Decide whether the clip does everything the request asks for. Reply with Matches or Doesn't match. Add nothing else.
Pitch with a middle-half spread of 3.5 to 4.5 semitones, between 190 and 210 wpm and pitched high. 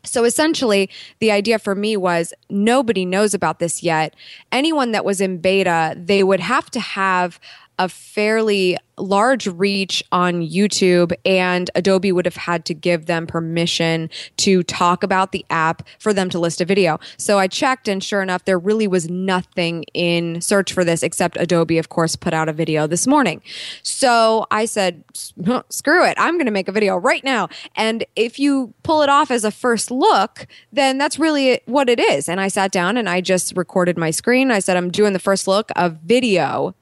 Matches